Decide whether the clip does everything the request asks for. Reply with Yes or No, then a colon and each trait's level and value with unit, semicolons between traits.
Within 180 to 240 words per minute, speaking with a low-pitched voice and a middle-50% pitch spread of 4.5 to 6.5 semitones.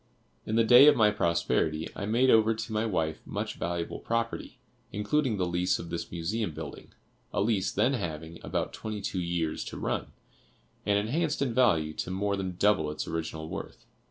Yes: average, 185 wpm; low, 100 Hz; average, 5.0 semitones